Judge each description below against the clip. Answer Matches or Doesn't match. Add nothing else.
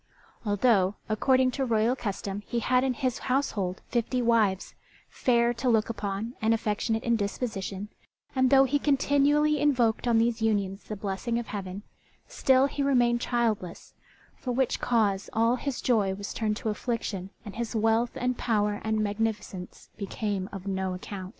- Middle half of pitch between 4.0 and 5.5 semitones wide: Doesn't match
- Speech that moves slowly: Doesn't match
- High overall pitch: Matches